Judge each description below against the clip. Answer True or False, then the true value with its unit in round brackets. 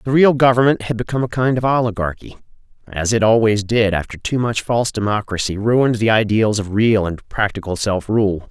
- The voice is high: False (110 Hz)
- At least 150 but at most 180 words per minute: False (190 wpm)